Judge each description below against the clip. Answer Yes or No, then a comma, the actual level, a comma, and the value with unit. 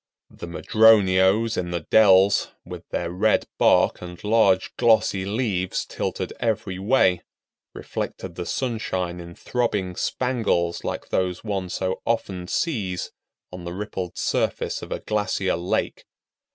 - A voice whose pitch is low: Yes, very low, 95 Hz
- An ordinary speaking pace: No, slow, 130 wpm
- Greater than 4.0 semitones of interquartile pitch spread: No, average, 3.5 semitones